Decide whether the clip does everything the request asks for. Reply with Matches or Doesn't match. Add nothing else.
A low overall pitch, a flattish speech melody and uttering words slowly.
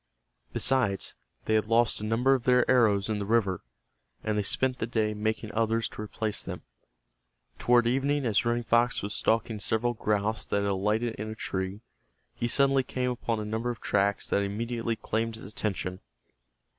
Doesn't match